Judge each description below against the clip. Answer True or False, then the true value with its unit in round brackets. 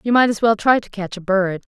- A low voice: False (205 Hz)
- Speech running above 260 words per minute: True (310 wpm)